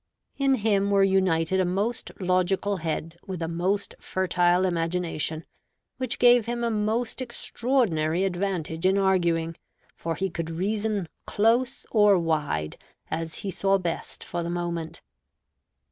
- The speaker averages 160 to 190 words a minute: No, slow, 135 wpm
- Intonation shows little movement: No, average, 3.8 semitones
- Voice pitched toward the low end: No, medium, 185 Hz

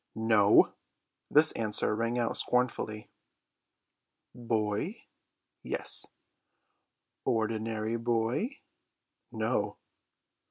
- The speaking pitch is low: Yes, low, 115 Hz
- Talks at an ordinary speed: No, slow, 65 wpm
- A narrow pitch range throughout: Yes, narrow, 1.8 semitones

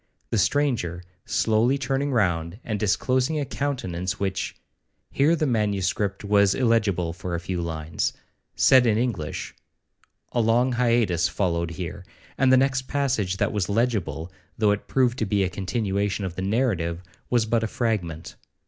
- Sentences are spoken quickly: No, average, 150 wpm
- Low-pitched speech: Yes, low, 105 Hz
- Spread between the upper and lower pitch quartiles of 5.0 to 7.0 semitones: Yes, average, 5.3 semitones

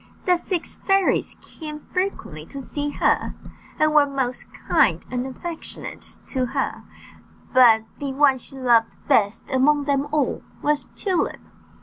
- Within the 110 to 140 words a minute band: Yes, slow, 135 wpm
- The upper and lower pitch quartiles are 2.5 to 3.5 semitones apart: Yes, average, 3.1 semitones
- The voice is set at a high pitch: Yes, very high, 280 Hz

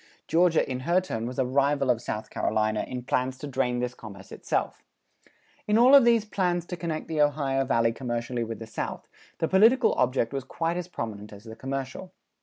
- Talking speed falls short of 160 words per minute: No, average, 200 wpm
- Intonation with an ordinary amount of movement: No, wide, 6.4 semitones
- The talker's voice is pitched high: No, low, 135 Hz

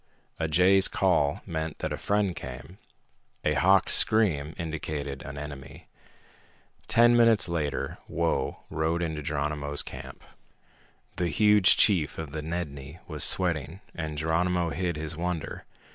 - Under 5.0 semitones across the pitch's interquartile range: Yes, average, 3.4 semitones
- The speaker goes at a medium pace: No, slow, 130 wpm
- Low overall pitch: Yes, very low, 80 Hz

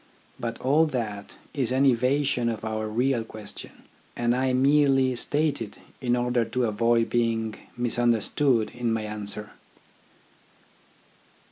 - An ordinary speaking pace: No, slow, 125 wpm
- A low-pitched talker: Yes, low, 120 Hz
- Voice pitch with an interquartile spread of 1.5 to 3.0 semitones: Yes, narrow, 2.6 semitones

